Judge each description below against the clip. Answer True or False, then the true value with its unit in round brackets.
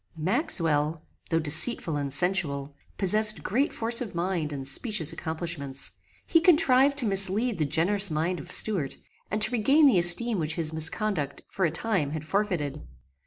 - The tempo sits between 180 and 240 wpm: False (160 wpm)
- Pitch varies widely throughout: True (5.8 semitones)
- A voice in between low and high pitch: True (175 Hz)